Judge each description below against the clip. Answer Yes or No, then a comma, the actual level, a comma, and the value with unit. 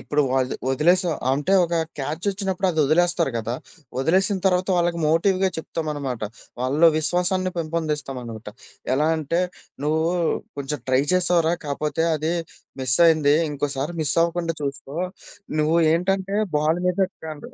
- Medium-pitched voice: Yes, medium, 160 Hz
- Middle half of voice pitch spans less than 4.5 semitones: Yes, average, 3.5 semitones